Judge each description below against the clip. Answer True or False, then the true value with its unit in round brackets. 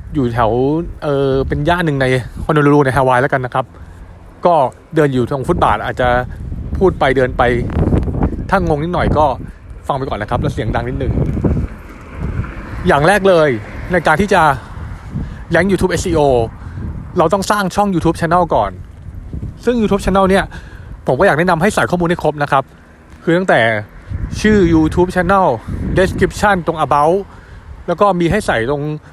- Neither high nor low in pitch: True (145 Hz)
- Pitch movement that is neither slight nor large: False (8.4 semitones)